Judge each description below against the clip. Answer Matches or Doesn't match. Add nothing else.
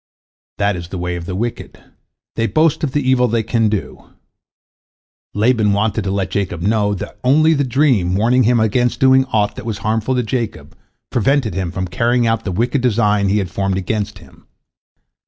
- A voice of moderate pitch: Doesn't match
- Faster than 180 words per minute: Matches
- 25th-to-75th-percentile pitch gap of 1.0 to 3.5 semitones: Doesn't match